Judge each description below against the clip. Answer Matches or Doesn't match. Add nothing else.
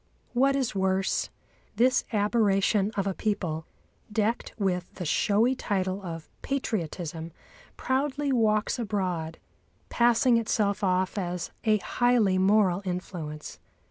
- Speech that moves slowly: Matches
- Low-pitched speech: Doesn't match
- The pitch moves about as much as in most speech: Matches